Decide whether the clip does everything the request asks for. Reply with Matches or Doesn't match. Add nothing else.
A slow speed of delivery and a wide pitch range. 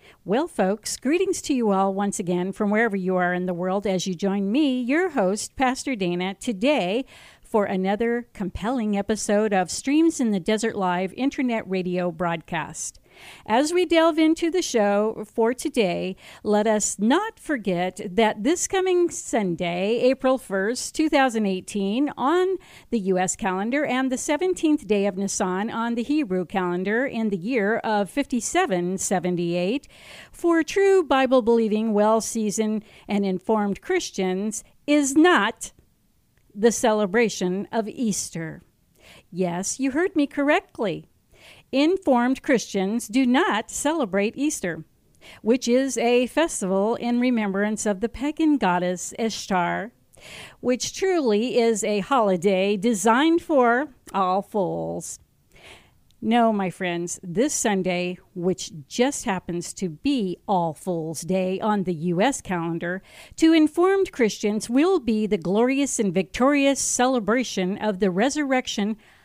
Matches